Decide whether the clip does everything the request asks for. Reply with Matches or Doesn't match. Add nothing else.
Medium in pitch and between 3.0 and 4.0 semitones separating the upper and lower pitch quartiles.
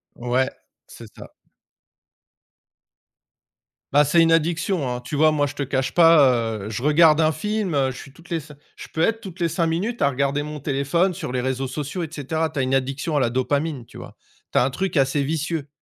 Matches